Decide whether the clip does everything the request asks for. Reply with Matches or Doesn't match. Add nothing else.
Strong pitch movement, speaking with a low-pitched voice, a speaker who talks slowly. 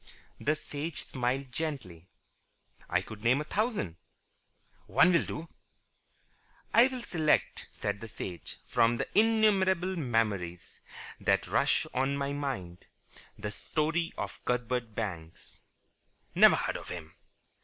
Matches